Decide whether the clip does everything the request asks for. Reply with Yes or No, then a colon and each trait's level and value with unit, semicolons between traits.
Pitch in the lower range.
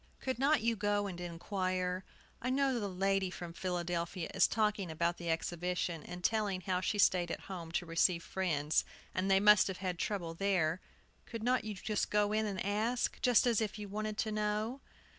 No: high, 195 Hz